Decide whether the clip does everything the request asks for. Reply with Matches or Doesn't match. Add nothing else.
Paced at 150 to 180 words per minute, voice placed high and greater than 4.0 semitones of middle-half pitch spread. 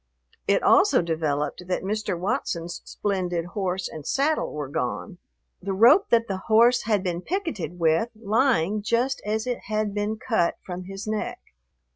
Matches